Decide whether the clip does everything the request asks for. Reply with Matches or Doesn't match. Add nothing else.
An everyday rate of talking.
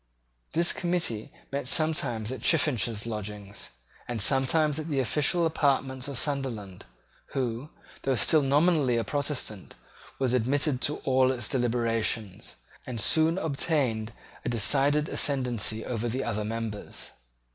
Doesn't match